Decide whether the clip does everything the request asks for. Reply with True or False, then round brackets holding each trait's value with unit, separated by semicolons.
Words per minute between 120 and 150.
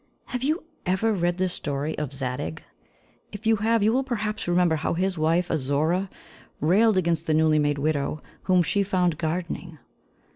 False (170 wpm)